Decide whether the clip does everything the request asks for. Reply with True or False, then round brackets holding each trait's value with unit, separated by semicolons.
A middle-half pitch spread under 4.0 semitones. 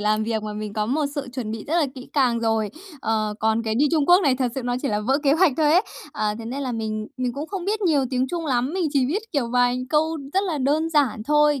False (5.2 semitones)